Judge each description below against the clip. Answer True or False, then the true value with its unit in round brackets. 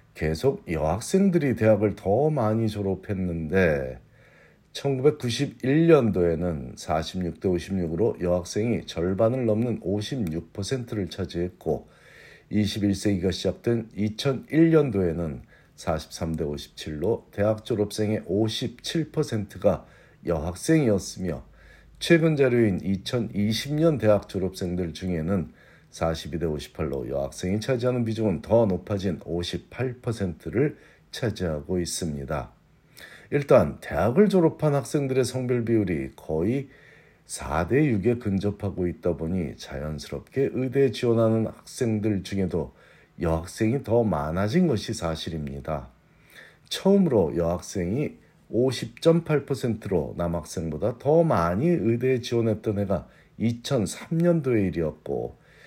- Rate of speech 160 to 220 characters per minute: True (215 characters per minute)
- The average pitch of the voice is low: True (105 Hz)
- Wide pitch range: True (6.4 semitones)